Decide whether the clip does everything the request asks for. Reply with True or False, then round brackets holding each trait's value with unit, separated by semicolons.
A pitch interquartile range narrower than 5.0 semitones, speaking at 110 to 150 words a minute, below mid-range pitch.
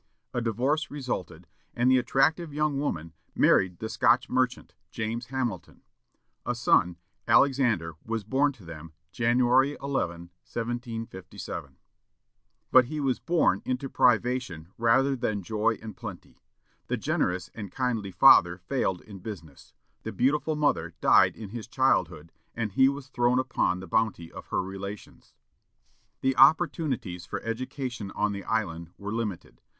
False (5.6 semitones; 140 wpm; 115 Hz)